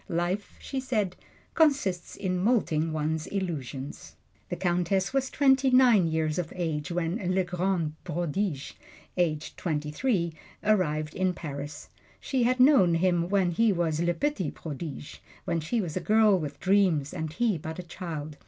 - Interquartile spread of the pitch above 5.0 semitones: No, average, 4.3 semitones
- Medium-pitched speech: Yes, medium, 175 Hz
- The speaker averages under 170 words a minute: Yes, average, 155 wpm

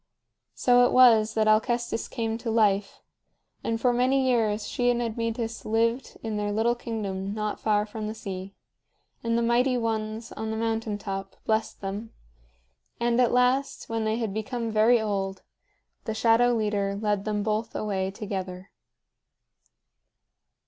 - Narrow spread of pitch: Yes, narrow, 2.1 semitones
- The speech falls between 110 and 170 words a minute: Yes, average, 150 wpm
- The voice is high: Yes, high, 220 Hz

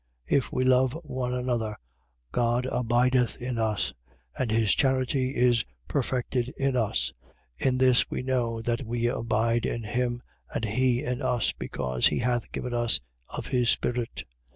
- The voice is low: Yes, low, 120 Hz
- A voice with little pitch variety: Yes, narrow, 1.7 semitones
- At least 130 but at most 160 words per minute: Yes, average, 155 wpm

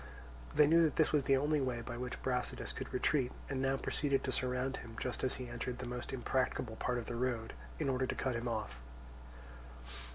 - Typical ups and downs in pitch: No, narrow, 1.9 semitones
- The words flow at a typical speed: No, fast, 215 wpm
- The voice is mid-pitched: No, low, 125 Hz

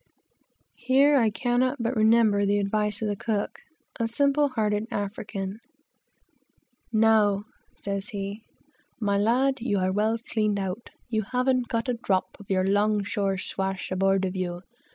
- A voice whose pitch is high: Yes, high, 210 Hz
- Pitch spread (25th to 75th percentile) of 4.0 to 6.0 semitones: No, average, 2.8 semitones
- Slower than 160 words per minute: Yes, average, 150 wpm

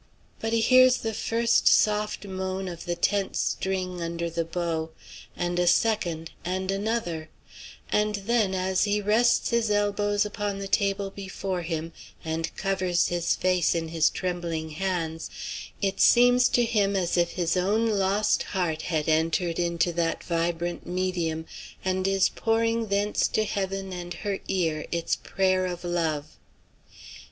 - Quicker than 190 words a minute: No, average, 150 wpm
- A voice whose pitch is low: No, medium, 185 Hz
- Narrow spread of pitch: No, average, 3.3 semitones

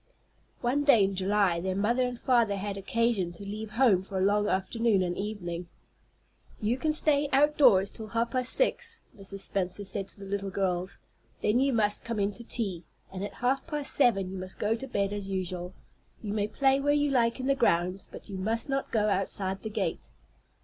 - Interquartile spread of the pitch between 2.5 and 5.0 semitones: Yes, average, 4.2 semitones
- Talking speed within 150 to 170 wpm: No, fast, 205 wpm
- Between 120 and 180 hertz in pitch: No, high, 210 Hz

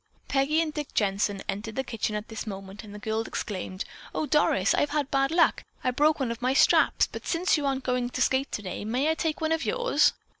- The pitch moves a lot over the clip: Yes, wide, 5.9 semitones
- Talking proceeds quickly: Yes, fast, 230 wpm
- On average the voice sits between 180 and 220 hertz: No, very high, 255 Hz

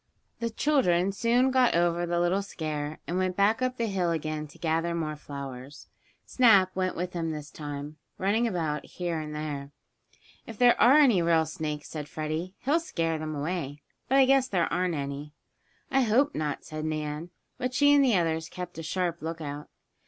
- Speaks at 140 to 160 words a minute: No, average, 185 wpm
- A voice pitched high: No, medium, 170 Hz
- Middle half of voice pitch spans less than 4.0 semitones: No, average, 5.0 semitones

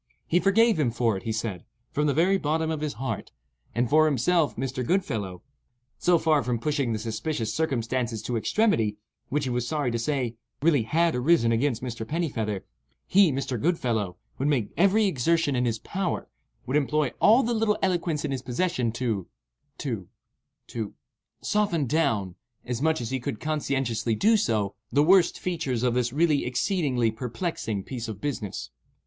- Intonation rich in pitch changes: Yes, wide, 5.7 semitones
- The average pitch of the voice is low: Yes, low, 130 Hz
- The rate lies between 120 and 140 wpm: No, average, 165 wpm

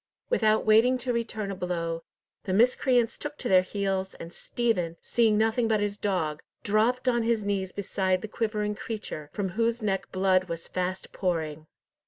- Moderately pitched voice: No, high, 205 Hz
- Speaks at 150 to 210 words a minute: Yes, average, 170 wpm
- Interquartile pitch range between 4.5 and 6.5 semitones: No, average, 3.6 semitones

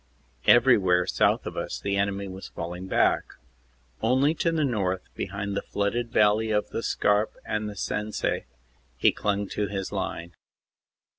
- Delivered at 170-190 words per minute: No, average, 150 wpm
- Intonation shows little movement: Yes, narrow, 2.2 semitones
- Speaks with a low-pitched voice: Yes, low, 100 Hz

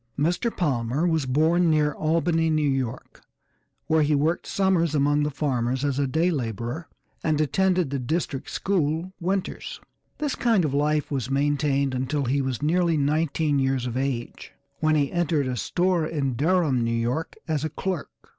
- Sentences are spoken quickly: No, average, 165 wpm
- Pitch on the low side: No, medium, 150 Hz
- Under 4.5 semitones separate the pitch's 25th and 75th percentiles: Yes, average, 3.5 semitones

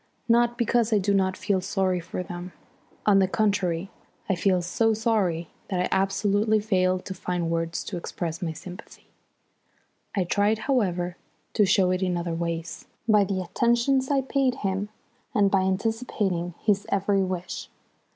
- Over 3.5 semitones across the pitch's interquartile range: No, average, 3.0 semitones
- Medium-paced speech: Yes, average, 160 wpm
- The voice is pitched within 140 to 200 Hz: Yes, high, 190 Hz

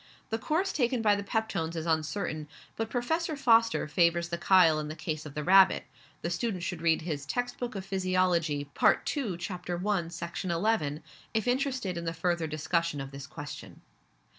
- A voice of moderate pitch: Yes, medium, 175 Hz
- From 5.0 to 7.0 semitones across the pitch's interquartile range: Yes, wide, 5.6 semitones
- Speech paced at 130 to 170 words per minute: No, average, 185 wpm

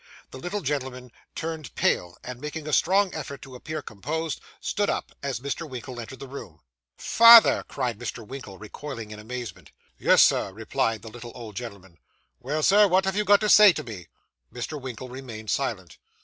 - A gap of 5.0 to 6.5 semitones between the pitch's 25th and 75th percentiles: Yes, wide, 5.5 semitones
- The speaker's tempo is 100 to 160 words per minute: No, average, 180 wpm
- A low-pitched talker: Yes, low, 130 Hz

